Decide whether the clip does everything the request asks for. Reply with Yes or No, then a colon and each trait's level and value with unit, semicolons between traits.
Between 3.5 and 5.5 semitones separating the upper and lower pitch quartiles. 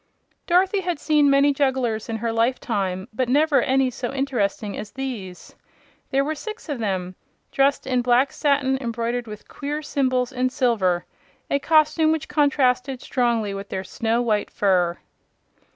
Yes: average, 4.1 semitones